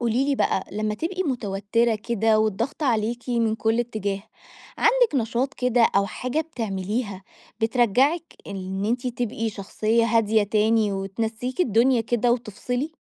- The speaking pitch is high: Yes, high, 230 Hz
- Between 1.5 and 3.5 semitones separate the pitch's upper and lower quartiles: Yes, average, 2.8 semitones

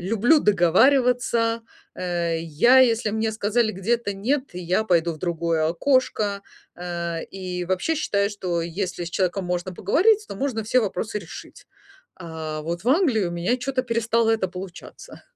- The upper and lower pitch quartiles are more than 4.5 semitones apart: Yes, average, 5.1 semitones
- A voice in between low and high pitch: No, high, 200 Hz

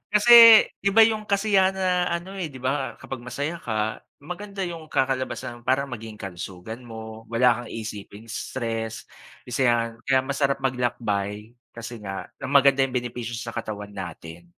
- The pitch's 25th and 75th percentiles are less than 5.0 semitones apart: No, wide, 5.6 semitones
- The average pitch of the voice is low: Yes, low, 125 Hz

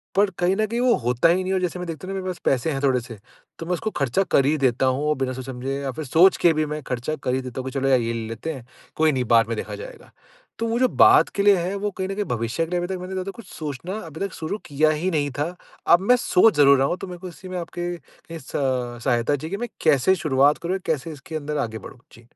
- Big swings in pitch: Yes, wide, 5.9 semitones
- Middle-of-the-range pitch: Yes, medium, 155 Hz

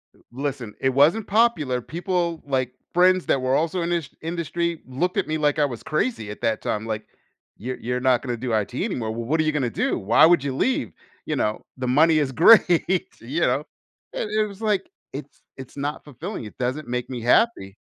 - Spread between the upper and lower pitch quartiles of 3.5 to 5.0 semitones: No, wide, 5.5 semitones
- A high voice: No, medium, 140 Hz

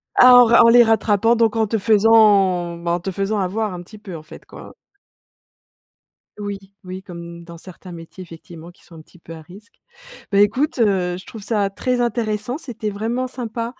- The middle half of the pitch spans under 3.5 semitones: No, average, 4.3 semitones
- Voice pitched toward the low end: No, high, 205 Hz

